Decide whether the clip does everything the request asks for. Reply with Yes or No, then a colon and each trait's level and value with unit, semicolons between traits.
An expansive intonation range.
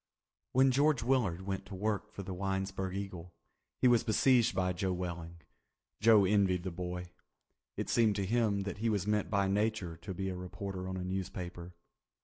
No: narrow, 2.6 semitones